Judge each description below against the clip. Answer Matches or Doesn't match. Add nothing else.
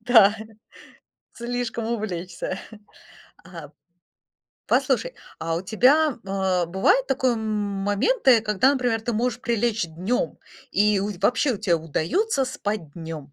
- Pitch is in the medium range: Doesn't match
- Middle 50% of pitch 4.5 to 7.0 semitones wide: Matches